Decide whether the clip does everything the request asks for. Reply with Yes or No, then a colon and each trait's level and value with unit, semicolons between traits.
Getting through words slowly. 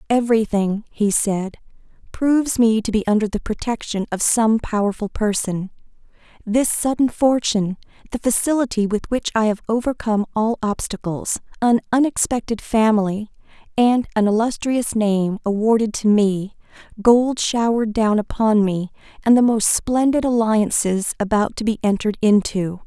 Yes: slow, 130 wpm